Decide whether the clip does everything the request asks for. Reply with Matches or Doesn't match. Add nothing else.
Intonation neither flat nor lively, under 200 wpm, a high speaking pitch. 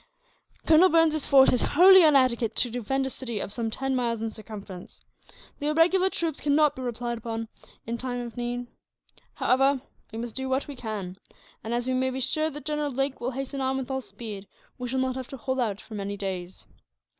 Doesn't match